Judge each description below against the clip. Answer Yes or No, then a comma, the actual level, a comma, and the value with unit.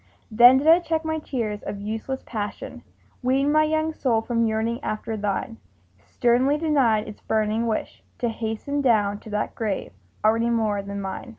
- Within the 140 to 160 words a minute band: No, average, 170 wpm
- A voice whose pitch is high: Yes, high, 230 Hz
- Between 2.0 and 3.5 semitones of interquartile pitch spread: No, average, 4.0 semitones